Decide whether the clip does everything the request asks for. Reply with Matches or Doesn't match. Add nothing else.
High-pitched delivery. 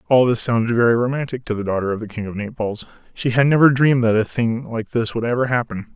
Doesn't match